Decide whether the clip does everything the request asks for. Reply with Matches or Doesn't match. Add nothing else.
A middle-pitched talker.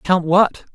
Matches